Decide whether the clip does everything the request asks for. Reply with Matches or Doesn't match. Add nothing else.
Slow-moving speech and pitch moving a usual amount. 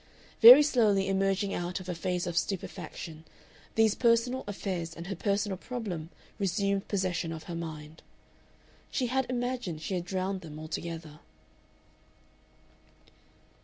Matches